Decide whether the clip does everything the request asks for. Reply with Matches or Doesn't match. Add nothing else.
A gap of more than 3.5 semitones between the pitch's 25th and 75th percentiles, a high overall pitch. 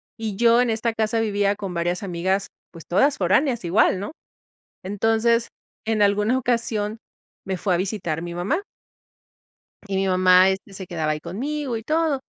Matches